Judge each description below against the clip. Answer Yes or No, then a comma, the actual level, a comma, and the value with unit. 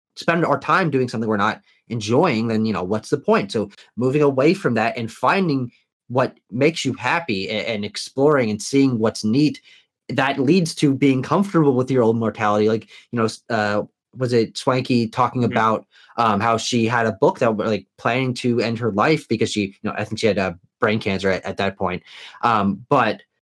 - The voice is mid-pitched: No, low, 115 Hz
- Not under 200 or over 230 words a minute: Yes, fast, 205 wpm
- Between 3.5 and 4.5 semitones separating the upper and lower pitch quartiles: Yes, average, 4.2 semitones